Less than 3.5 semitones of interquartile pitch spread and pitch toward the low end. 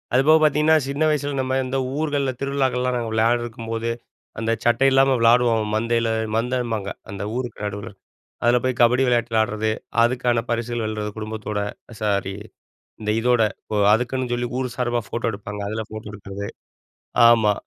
Yes: narrow, 2.6 semitones; low, 120 Hz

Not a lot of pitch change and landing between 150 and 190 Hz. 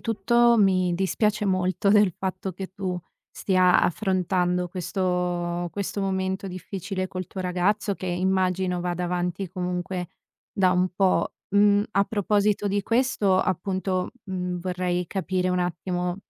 Yes: narrow, 1.5 semitones; medium, 185 Hz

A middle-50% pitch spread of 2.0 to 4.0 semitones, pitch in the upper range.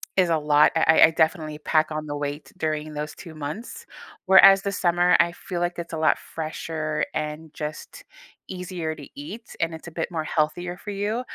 No: average, 2.7 semitones; medium, 160 Hz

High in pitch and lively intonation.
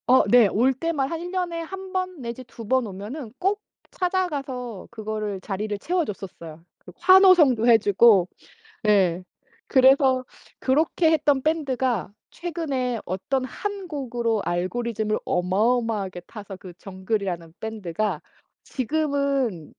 Yes: high, 245 Hz; wide, 6.7 semitones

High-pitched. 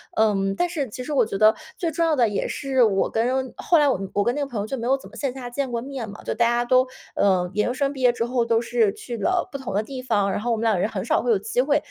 Yes: high, 240 Hz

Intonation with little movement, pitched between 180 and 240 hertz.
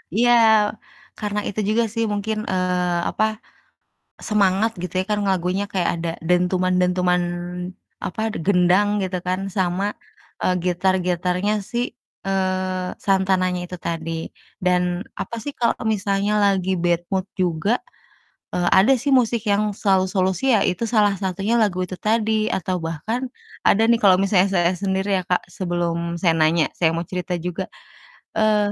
Yes: narrow, 2.2 semitones; medium, 185 Hz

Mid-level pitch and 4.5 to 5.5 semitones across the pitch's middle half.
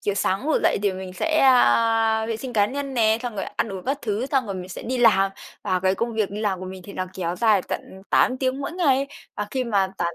No: high, 220 Hz; average, 4.9 semitones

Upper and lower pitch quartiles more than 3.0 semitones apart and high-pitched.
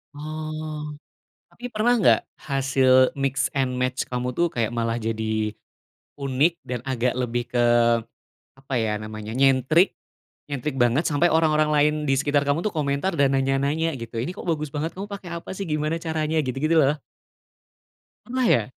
No: average, 3.7 semitones; medium, 140 Hz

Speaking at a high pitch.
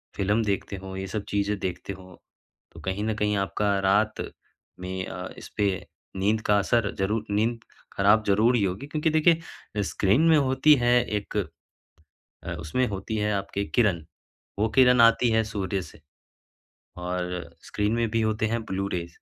No: low, 105 Hz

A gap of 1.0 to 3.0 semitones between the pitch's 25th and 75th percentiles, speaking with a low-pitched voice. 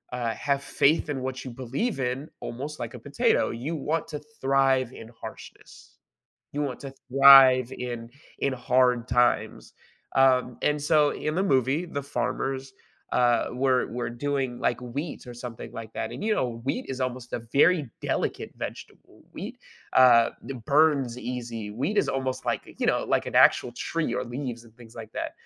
Yes: narrow, 2.5 semitones; low, 130 Hz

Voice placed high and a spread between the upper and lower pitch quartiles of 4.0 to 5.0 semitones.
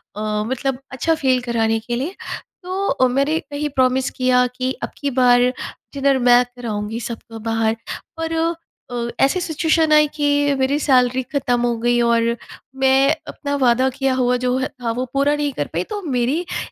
No: very high, 255 Hz; average, 2.9 semitones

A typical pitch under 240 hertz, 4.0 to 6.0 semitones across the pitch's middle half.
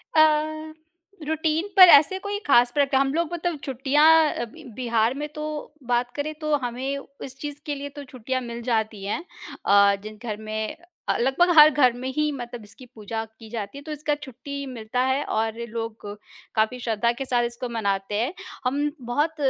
No: very high, 255 Hz; average, 4.4 semitones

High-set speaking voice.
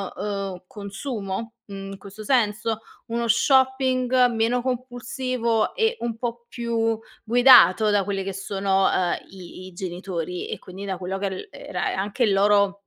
Yes: high, 210 Hz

